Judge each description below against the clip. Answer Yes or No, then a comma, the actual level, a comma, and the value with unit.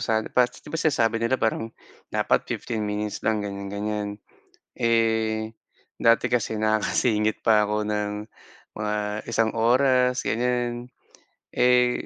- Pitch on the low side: Yes, low, 115 Hz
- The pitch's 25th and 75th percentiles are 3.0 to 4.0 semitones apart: No, narrow, 2.5 semitones